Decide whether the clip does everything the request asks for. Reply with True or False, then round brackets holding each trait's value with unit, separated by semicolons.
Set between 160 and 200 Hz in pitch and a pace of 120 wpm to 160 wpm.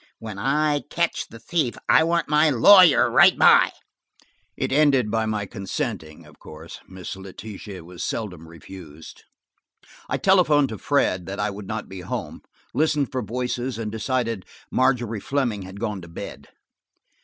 False (115 Hz; 155 wpm)